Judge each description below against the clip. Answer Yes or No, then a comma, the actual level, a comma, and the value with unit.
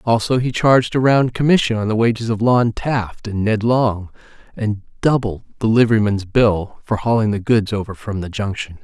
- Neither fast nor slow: Yes, average, 190 wpm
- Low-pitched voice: Yes, low, 110 Hz